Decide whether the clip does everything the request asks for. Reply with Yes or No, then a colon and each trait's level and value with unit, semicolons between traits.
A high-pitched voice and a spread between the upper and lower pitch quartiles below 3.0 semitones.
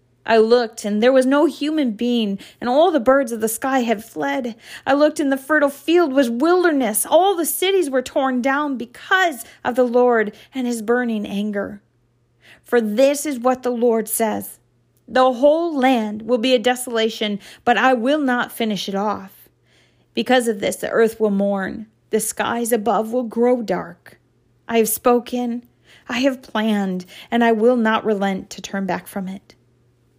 No: high, 240 Hz; average, 4.0 semitones